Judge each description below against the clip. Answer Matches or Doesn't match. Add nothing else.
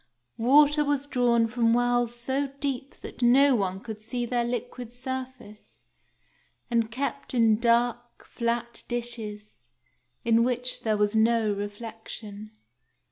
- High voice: Matches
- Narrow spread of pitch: Matches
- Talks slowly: Matches